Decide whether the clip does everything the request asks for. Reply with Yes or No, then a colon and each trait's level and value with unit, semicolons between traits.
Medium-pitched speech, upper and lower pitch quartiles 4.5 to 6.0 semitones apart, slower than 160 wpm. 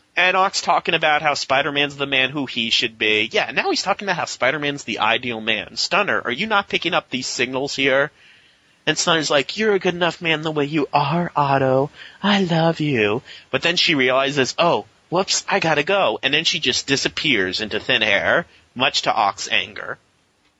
No: medium, 145 Hz; average, 4.8 semitones; fast, 205 wpm